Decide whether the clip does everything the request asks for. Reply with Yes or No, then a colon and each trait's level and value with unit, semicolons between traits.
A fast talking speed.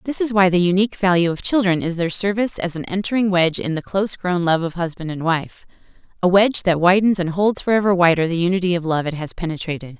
Yes: fast, 235 wpm